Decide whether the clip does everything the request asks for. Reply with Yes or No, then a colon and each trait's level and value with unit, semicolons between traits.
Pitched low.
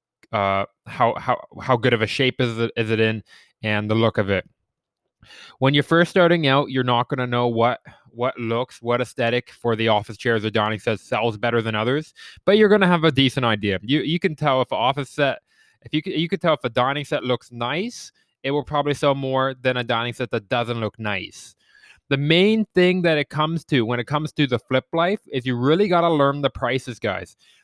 Yes: low, 130 Hz